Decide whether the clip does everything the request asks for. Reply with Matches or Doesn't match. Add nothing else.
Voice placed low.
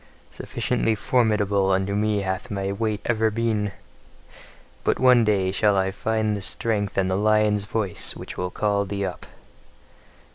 Matches